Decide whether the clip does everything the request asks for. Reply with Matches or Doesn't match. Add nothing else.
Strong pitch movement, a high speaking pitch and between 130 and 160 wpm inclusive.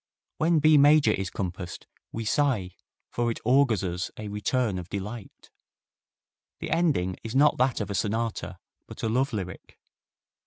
Doesn't match